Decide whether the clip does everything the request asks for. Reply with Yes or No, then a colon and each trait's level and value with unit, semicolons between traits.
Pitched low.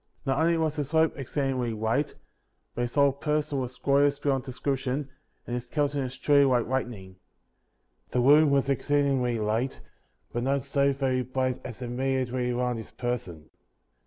Yes: low, 130 Hz